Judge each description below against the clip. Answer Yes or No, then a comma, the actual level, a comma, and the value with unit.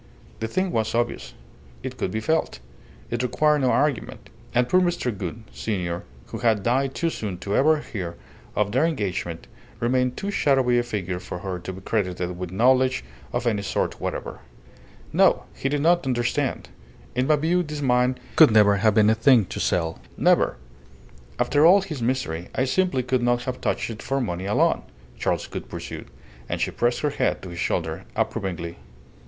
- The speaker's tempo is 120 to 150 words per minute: No, average, 180 wpm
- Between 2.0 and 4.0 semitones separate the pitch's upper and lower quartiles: No, wide, 5.5 semitones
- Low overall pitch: Yes, low, 120 Hz